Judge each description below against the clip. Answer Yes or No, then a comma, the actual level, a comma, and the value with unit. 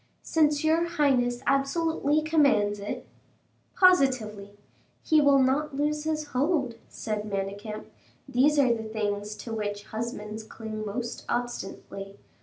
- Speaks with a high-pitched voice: Yes, high, 245 Hz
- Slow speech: Yes, slow, 120 wpm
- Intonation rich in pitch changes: Yes, wide, 5.8 semitones